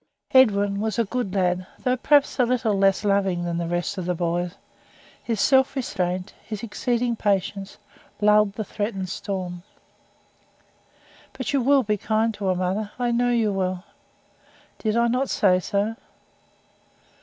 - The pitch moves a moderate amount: Yes, average, 4.1 semitones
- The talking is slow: No, average, 155 wpm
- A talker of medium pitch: No, high, 205 Hz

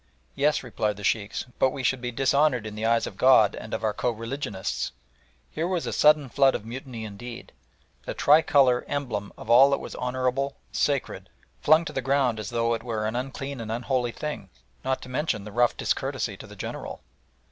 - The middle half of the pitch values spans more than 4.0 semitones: No, average, 3.4 semitones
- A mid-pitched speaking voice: No, low, 125 Hz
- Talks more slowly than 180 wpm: No, average, 200 wpm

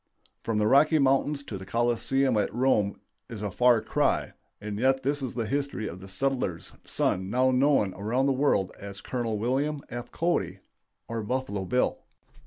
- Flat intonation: No, average, 4.5 semitones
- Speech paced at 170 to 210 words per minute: Yes, average, 175 wpm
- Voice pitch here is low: Yes, low, 120 Hz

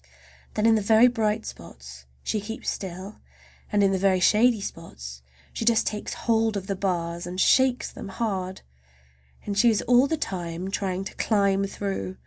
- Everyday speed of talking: Yes, average, 175 wpm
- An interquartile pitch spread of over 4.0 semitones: No, average, 3.2 semitones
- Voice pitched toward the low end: No, high, 200 Hz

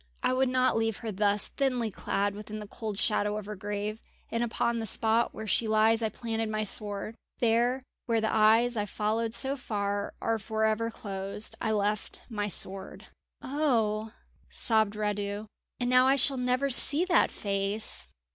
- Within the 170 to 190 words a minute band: Yes, average, 175 wpm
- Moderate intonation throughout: No, narrow, 2.2 semitones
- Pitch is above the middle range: Yes, high, 220 Hz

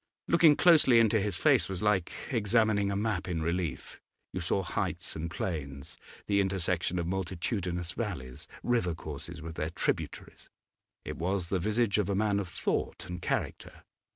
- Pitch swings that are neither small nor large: Yes, average, 3.7 semitones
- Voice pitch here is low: Yes, very low, 95 Hz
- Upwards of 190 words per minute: No, average, 160 wpm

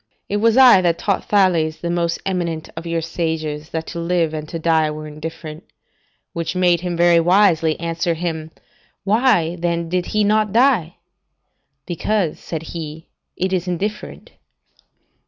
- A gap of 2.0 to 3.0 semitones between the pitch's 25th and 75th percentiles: Yes, narrow, 2.4 semitones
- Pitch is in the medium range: Yes, medium, 170 Hz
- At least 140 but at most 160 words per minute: Yes, average, 155 wpm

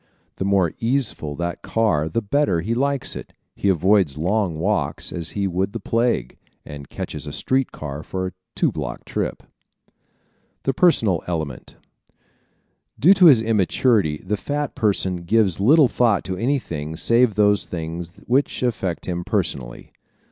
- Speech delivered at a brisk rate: No, average, 155 wpm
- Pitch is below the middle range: Yes, low, 100 Hz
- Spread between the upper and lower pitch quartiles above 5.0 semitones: Yes, wide, 5.6 semitones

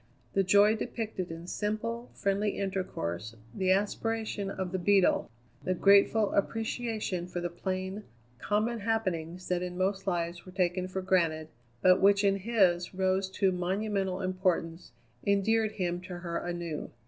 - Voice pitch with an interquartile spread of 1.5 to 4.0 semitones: Yes, narrow, 2.4 semitones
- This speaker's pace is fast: No, average, 145 wpm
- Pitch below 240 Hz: Yes, high, 190 Hz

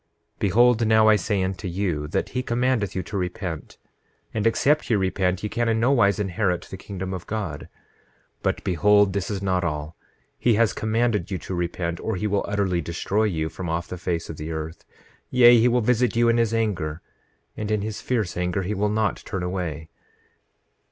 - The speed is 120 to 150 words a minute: No, average, 195 wpm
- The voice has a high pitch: No, low, 100 Hz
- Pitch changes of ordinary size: Yes, average, 3.8 semitones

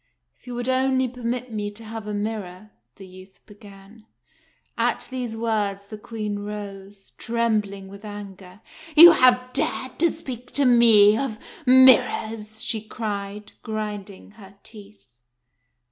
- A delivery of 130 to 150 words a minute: Yes, average, 140 wpm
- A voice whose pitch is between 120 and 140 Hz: No, high, 215 Hz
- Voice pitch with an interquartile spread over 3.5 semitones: No, average, 3.0 semitones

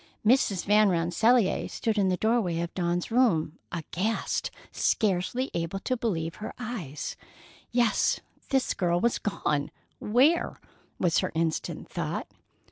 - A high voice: Yes, high, 195 Hz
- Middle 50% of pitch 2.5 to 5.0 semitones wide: No, wide, 5.4 semitones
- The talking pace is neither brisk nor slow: No, slow, 125 wpm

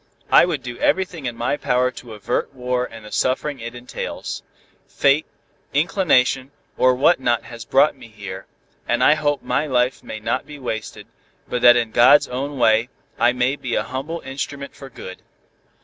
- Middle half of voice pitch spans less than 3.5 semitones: Yes, average, 2.8 semitones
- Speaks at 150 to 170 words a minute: No, average, 180 wpm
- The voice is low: Yes, low, 125 Hz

